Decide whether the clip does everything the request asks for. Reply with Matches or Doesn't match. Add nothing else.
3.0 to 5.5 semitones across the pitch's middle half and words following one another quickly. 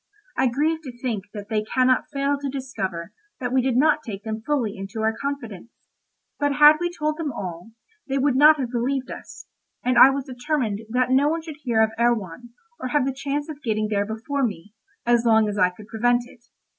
Matches